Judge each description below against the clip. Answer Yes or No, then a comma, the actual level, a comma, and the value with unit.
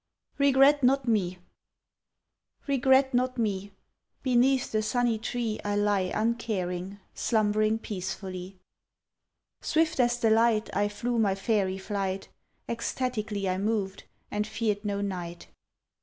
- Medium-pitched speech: No, high, 215 Hz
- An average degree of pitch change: Yes, average, 3.7 semitones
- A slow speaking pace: Yes, slow, 115 wpm